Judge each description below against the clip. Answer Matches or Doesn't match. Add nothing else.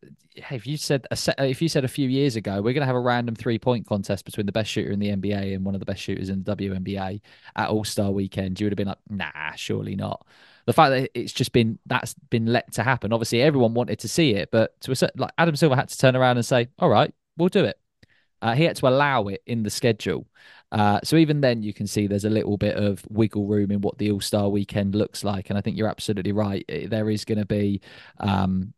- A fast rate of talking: Matches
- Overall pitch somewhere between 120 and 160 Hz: Doesn't match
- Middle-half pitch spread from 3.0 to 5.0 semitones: Matches